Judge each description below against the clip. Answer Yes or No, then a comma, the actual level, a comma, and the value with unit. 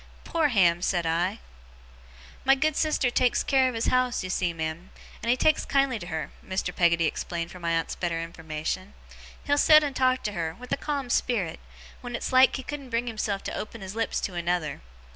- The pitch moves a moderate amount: No, wide, 7.1 semitones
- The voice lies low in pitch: No, high, 205 Hz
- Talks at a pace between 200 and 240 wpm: Yes, fast, 205 wpm